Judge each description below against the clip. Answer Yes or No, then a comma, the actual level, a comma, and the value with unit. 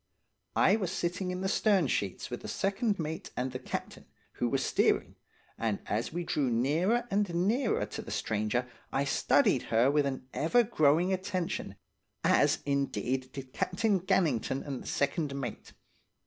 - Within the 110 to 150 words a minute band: No, average, 160 wpm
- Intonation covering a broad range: Yes, wide, 6.5 semitones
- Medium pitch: Yes, medium, 150 Hz